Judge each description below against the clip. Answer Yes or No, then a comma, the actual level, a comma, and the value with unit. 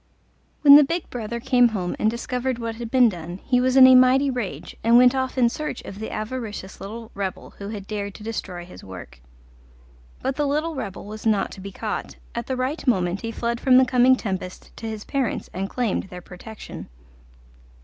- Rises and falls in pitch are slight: No, average, 4.3 semitones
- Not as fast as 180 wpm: No, fast, 205 wpm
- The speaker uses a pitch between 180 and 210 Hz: No, high, 230 Hz